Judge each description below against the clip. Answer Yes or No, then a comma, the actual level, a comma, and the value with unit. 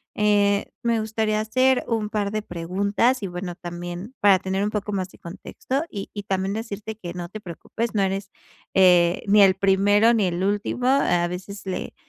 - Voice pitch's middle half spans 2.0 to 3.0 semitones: Yes, narrow, 2.5 semitones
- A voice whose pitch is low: No, high, 200 Hz